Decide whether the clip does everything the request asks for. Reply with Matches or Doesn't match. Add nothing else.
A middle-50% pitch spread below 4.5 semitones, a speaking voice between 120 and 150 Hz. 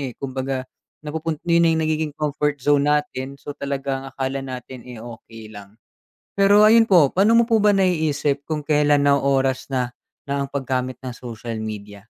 Matches